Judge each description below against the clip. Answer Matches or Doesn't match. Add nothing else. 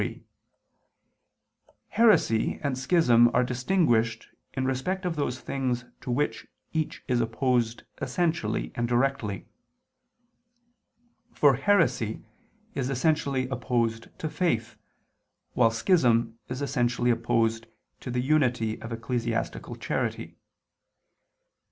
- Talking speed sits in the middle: Doesn't match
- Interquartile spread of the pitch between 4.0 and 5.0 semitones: Doesn't match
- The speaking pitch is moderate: Doesn't match